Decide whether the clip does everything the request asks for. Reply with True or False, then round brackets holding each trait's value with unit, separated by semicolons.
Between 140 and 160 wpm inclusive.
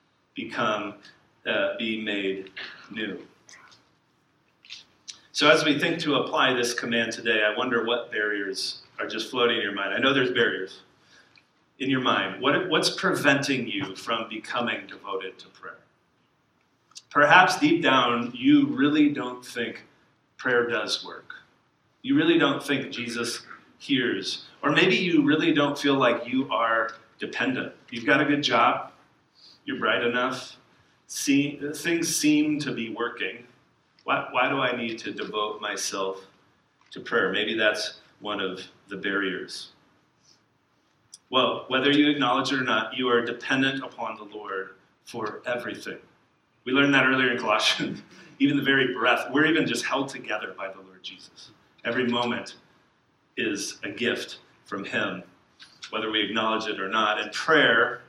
True (150 wpm)